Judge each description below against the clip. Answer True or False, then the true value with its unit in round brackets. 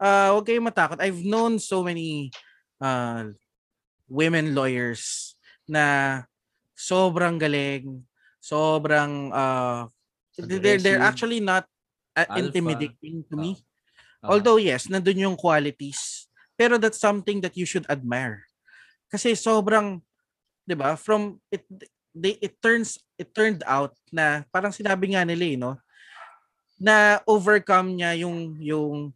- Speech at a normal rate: True (120 wpm)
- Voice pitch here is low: False (175 Hz)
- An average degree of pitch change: False (6.0 semitones)